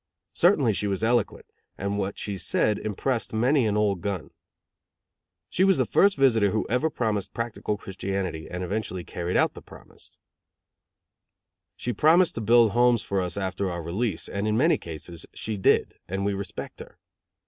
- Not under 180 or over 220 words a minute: No, average, 170 wpm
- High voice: No, low, 105 Hz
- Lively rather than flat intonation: No, average, 3.8 semitones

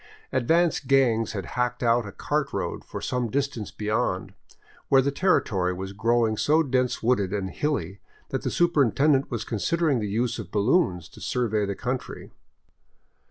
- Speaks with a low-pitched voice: Yes, low, 120 Hz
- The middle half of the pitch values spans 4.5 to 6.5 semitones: Yes, average, 4.8 semitones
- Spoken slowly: No, average, 160 wpm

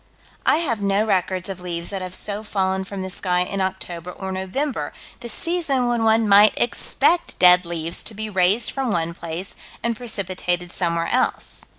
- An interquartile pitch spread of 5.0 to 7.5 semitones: No, average, 3.6 semitones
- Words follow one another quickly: No, average, 180 wpm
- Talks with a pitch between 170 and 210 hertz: Yes, high, 190 Hz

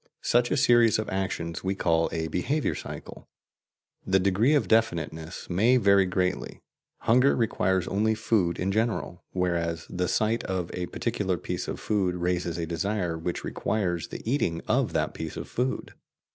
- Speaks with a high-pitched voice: No, very low, 95 Hz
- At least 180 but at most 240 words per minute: No, average, 160 wpm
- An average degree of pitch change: Yes, average, 4.2 semitones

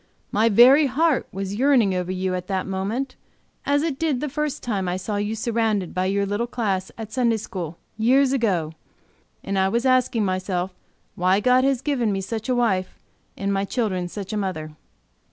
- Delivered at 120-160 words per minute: No, average, 190 wpm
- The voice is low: No, high, 210 Hz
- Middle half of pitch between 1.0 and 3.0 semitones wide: No, average, 4.9 semitones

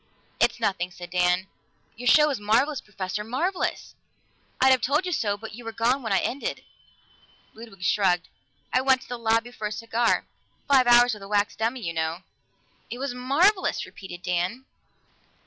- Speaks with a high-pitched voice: Yes, high, 230 Hz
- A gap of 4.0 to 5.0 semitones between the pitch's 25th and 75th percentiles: Yes, average, 4.7 semitones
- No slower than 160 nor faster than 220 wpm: Yes, average, 175 wpm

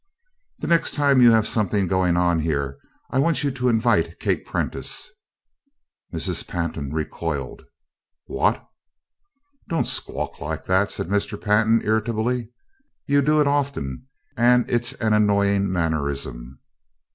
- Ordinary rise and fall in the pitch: No, wide, 6.6 semitones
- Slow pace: Yes, slow, 130 wpm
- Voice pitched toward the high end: No, low, 105 Hz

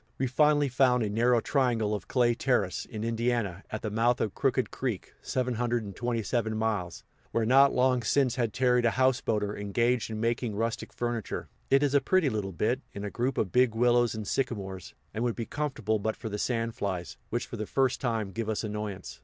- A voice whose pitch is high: No, low, 115 Hz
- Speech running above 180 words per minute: Yes, average, 195 wpm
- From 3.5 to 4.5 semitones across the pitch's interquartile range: No, average, 2.7 semitones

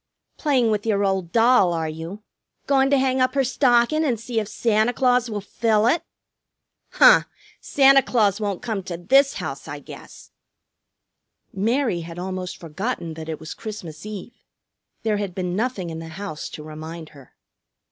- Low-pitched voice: No, high, 210 Hz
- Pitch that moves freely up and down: Yes, wide, 6.2 semitones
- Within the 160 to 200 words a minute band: Yes, average, 165 wpm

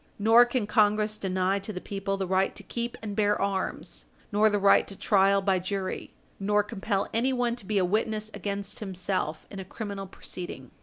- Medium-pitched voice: No, high, 200 Hz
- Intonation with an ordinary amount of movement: No, narrow, 1.9 semitones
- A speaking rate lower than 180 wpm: No, average, 190 wpm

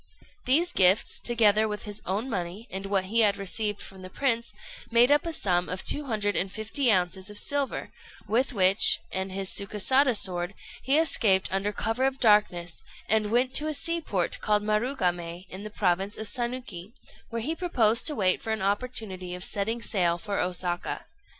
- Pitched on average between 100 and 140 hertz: No, high, 210 Hz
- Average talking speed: Yes, average, 180 wpm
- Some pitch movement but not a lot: Yes, average, 4.1 semitones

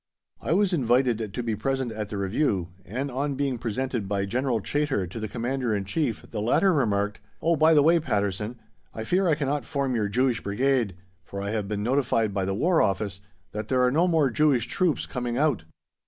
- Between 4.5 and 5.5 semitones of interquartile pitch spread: Yes, average, 5.2 semitones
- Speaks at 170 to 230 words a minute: Yes, fast, 205 wpm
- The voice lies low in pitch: Yes, low, 120 Hz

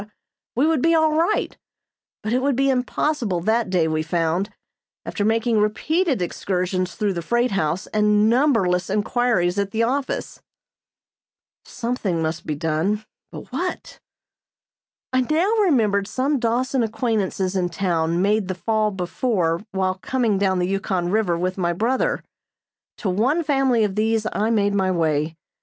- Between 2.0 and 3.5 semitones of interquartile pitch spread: No, average, 5.1 semitones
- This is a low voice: No, high, 210 Hz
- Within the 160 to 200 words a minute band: No, average, 150 wpm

